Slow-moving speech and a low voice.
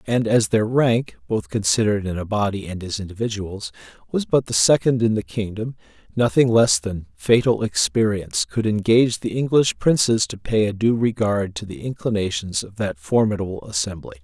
No: average, 175 wpm; low, 110 Hz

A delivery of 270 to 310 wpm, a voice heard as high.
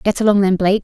Yes: fast, 290 wpm; high, 200 Hz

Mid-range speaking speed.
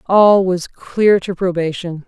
Yes: average, 145 wpm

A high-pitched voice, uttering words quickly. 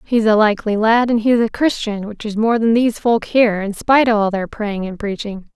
Yes: high, 220 Hz; fast, 250 wpm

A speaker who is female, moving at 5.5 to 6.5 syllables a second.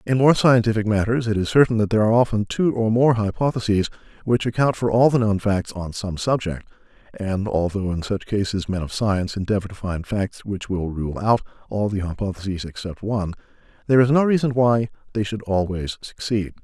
No: male; 5.6 syllables/s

